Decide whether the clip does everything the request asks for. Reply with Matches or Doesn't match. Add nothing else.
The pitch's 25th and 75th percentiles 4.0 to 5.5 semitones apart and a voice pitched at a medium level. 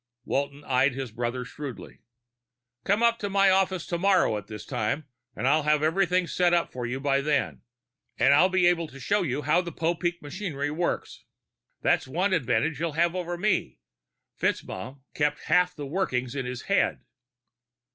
Matches